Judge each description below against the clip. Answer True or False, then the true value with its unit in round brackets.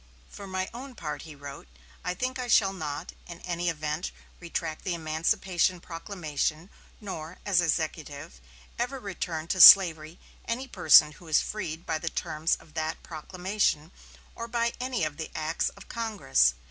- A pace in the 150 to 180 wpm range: True (160 wpm)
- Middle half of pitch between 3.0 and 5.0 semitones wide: True (4.2 semitones)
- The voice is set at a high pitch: False (170 Hz)